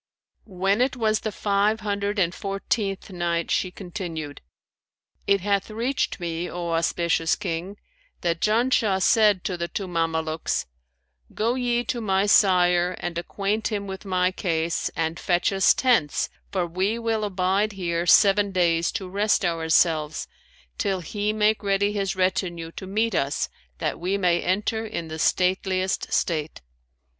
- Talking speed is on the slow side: No, average, 150 wpm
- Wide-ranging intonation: No, average, 3.3 semitones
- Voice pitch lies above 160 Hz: Yes, high, 190 Hz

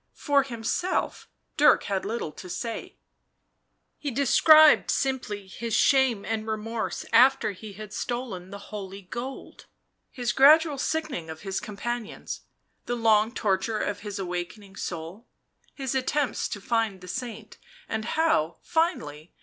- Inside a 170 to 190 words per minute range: No, slow, 135 wpm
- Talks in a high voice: Yes, high, 225 Hz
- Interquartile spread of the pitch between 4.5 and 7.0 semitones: Yes, average, 4.9 semitones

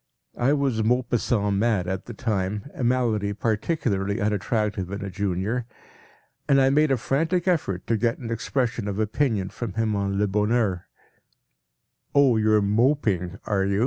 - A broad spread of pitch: No, average, 3.6 semitones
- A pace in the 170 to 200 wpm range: No, average, 155 wpm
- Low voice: Yes, low, 110 Hz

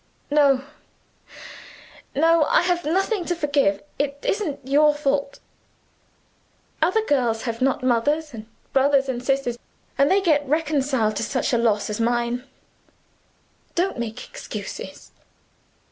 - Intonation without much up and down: No, average, 4.0 semitones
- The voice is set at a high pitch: Yes, very high, 275 Hz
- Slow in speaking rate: Yes, slow, 120 wpm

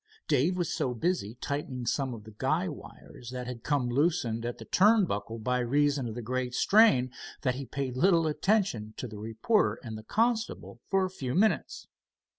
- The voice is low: Yes, low, 130 Hz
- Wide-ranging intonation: Yes, wide, 6.4 semitones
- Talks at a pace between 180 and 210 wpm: Yes, average, 190 wpm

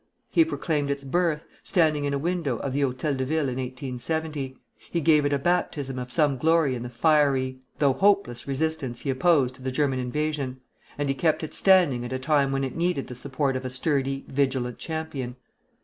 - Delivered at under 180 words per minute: No, average, 200 wpm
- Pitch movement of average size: Yes, average, 3.3 semitones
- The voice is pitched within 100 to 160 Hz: Yes, medium, 140 Hz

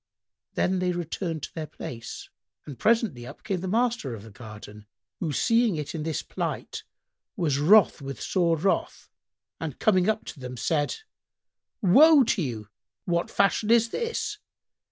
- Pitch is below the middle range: No, medium, 170 Hz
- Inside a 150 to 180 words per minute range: Yes, average, 155 wpm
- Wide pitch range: Yes, wide, 7.9 semitones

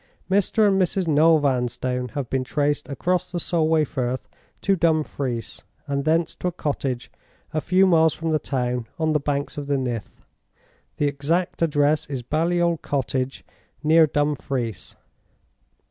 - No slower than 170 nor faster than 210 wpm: No, average, 145 wpm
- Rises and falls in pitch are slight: No, average, 3.7 semitones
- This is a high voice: No, medium, 150 Hz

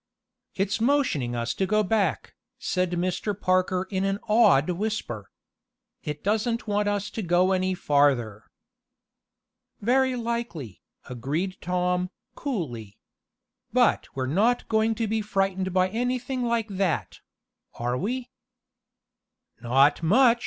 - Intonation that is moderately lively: No, wide, 5.8 semitones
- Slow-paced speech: Yes, slow, 120 wpm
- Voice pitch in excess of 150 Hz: Yes, high, 190 Hz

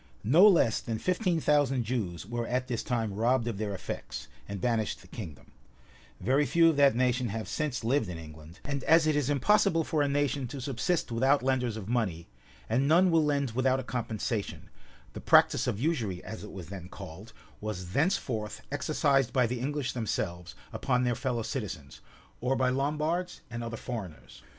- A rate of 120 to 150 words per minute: No, average, 185 wpm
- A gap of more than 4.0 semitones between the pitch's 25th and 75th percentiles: Yes, average, 4.8 semitones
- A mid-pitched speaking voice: No, low, 125 Hz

